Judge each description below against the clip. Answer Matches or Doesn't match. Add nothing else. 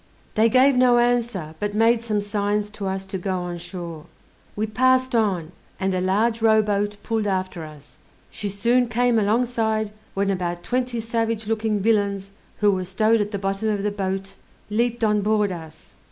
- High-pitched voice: Matches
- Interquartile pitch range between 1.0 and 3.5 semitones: Matches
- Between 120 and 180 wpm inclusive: Matches